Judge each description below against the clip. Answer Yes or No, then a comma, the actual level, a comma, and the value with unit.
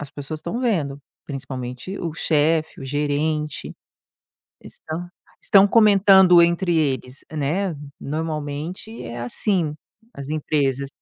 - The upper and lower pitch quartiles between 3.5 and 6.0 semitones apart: Yes, average, 3.9 semitones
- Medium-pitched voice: Yes, medium, 155 Hz